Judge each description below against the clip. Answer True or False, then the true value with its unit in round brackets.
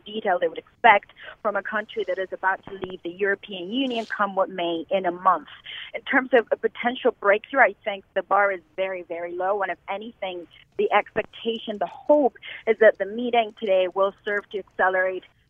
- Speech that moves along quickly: False (195 wpm)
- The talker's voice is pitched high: True (200 Hz)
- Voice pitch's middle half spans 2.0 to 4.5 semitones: True (3.0 semitones)